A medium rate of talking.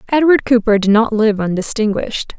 Yes: average, 150 wpm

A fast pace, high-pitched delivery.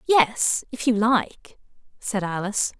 No: slow, 130 wpm; high, 220 Hz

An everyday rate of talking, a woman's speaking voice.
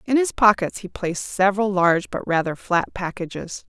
Yes: average, 175 wpm; female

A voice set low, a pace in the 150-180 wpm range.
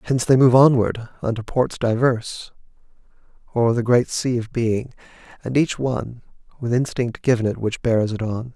Yes: low, 120 Hz; average, 170 wpm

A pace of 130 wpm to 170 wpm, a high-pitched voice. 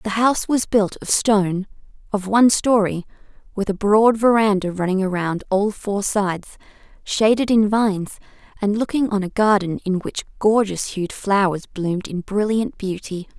Yes: average, 155 wpm; high, 205 Hz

